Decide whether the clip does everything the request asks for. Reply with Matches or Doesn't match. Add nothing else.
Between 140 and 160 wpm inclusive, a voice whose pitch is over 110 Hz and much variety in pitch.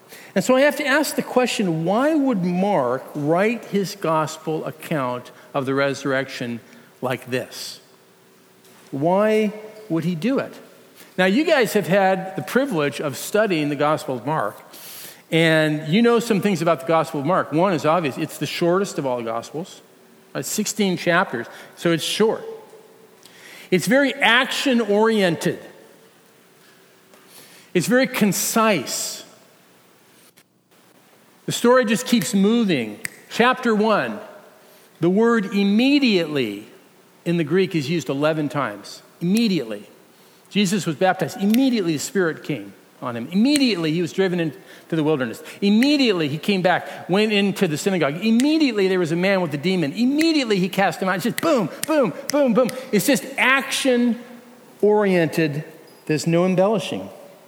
Matches